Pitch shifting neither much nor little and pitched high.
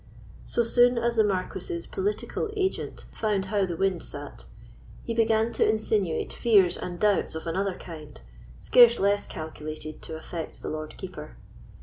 No: wide, 5.9 semitones; high, 200 Hz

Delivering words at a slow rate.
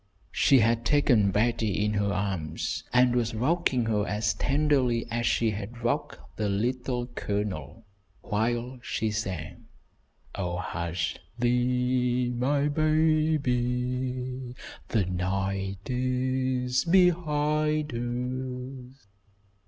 Yes: slow, 100 wpm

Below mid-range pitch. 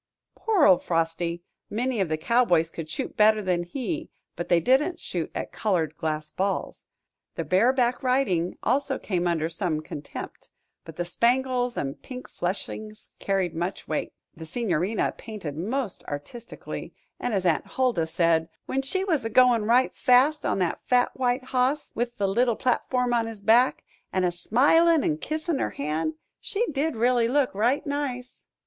No: high, 225 Hz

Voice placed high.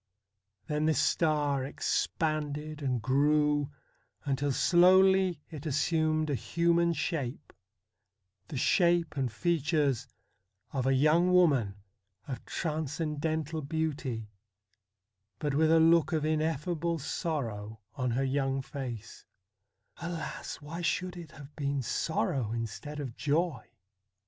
No: medium, 150 Hz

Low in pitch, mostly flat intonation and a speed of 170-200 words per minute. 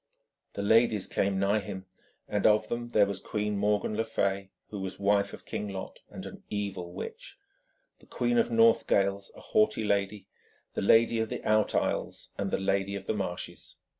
Yes: low, 100 Hz; narrow, 2.1 semitones; average, 185 wpm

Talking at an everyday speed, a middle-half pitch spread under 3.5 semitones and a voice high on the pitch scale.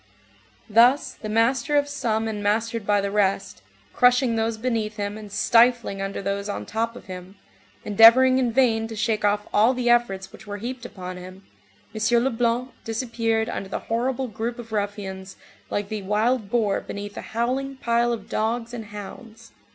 Yes: average, 175 wpm; average, 2.7 semitones; high, 225 Hz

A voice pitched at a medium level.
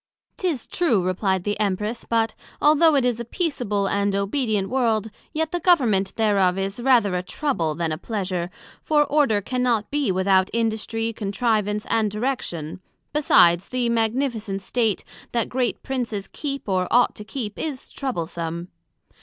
No: high, 220 Hz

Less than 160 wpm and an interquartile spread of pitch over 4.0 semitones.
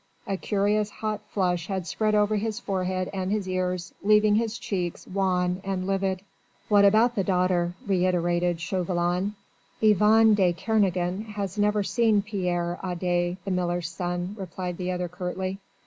No: average, 150 wpm; narrow, 2.5 semitones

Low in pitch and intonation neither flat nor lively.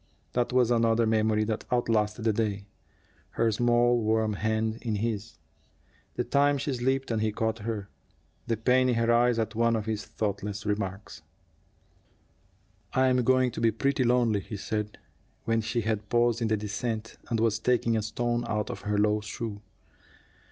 No: low, 115 Hz; narrow, 2.0 semitones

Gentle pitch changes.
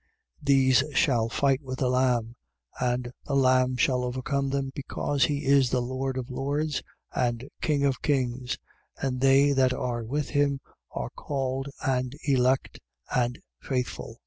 Yes: narrow, 1.7 semitones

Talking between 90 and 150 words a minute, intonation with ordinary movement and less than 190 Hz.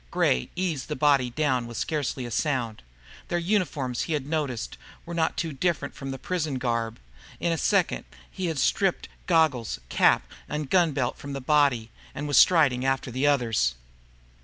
No: average, 175 wpm; average, 4.4 semitones; medium, 140 Hz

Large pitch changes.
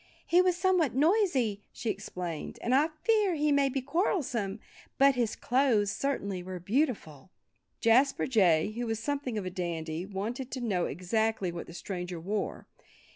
Yes: wide, 6.9 semitones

